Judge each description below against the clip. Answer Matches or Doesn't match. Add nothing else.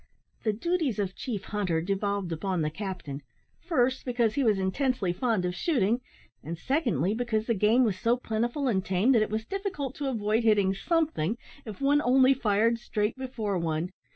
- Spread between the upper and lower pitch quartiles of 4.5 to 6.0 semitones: Matches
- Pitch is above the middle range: Matches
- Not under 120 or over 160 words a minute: Doesn't match